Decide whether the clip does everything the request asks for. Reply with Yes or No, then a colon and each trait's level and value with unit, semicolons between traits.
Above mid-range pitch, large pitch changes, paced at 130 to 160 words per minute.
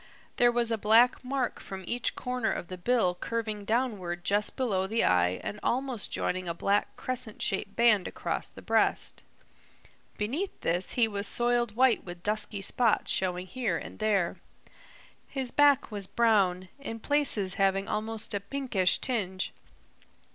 No: high, 215 Hz; average, 4.1 semitones; average, 155 wpm